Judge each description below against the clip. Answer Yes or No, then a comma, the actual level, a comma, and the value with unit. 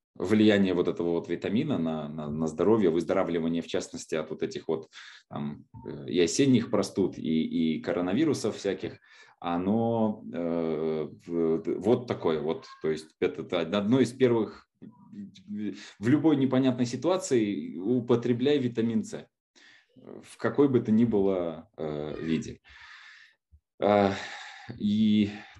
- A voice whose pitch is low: Yes, low, 105 Hz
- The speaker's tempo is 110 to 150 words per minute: Yes, average, 125 wpm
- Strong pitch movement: Yes, wide, 7.0 semitones